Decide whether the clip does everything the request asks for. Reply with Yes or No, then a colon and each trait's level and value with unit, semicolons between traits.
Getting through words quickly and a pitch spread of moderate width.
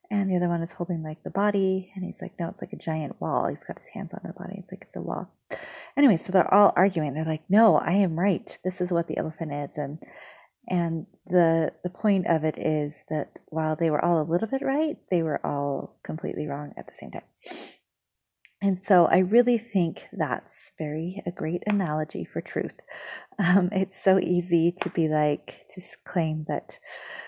Yes: fast, 210 wpm; average, 3.4 semitones